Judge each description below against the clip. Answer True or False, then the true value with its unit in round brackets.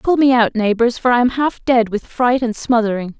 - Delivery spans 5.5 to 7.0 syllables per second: False (5.2 syllables/s)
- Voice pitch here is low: False (235 Hz)